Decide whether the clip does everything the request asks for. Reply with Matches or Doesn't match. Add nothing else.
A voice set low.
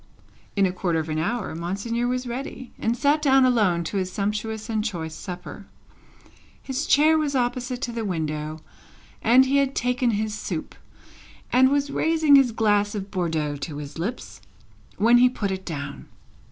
Doesn't match